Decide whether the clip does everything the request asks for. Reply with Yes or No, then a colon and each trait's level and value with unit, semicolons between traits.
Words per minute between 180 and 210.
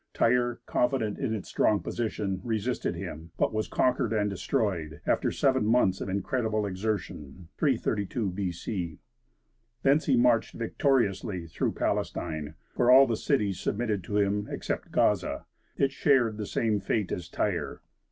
No: average, 140 wpm